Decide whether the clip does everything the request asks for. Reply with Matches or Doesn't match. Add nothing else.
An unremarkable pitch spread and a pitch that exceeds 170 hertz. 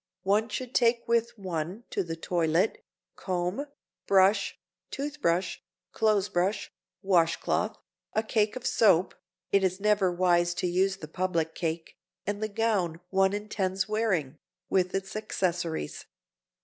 Matches